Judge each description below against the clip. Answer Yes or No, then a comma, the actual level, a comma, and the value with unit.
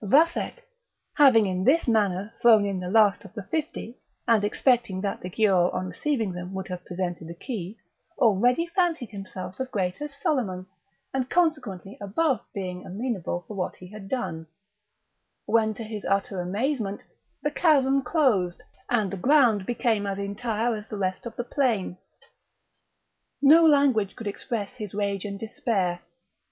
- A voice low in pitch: No, high, 210 Hz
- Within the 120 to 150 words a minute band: No, average, 160 wpm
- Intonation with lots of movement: No, average, 4.9 semitones